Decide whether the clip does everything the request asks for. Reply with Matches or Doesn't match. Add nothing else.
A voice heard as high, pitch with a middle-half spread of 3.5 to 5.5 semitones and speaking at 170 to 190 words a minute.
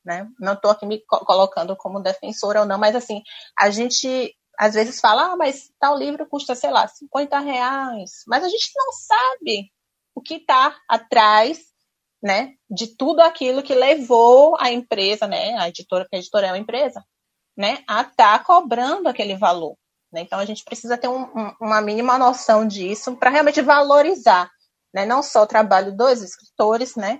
Matches